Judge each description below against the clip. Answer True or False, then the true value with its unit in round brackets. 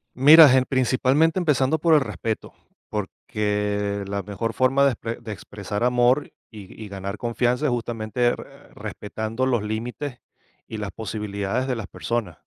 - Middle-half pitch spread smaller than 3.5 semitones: False (3.8 semitones)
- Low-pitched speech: True (115 Hz)